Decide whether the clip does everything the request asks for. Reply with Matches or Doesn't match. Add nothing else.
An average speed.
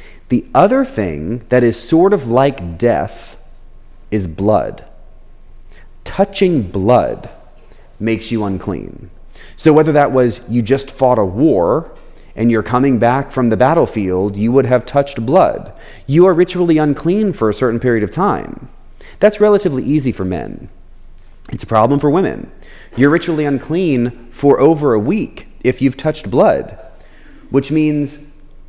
Matches